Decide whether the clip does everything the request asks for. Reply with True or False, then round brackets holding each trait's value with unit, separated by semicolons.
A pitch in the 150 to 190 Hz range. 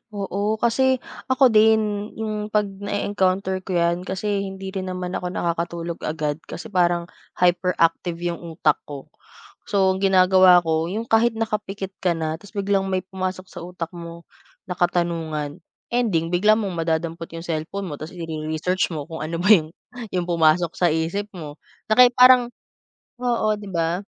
True (185 Hz)